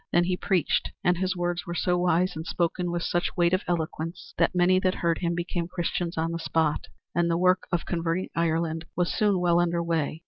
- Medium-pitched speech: Yes, medium, 175 Hz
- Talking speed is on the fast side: Yes, fast, 215 wpm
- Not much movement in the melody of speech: Yes, narrow, 1.2 semitones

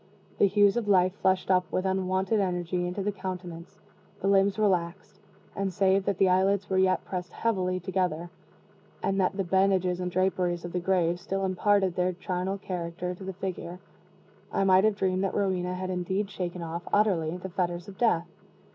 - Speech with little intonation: Yes, narrow, 1.4 semitones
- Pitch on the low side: No, medium, 185 Hz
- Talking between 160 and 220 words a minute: Yes, average, 180 wpm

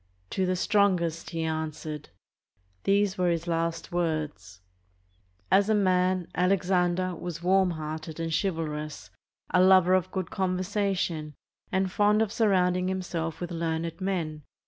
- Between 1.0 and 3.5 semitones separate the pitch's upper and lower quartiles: Yes, narrow, 2.6 semitones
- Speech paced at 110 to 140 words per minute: Yes, slow, 135 wpm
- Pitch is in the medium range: Yes, medium, 180 Hz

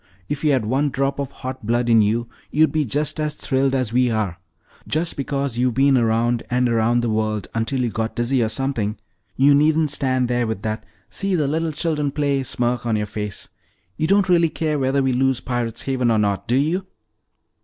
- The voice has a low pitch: Yes, low, 130 Hz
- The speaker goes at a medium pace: No, fast, 210 wpm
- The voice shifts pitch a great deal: No, average, 3.9 semitones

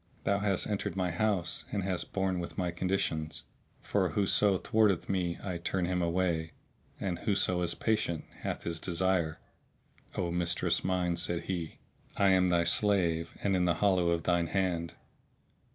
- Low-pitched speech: Yes, very low, 90 Hz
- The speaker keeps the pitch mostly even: Yes, narrow, 2.1 semitones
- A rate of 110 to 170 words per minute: Yes, average, 160 wpm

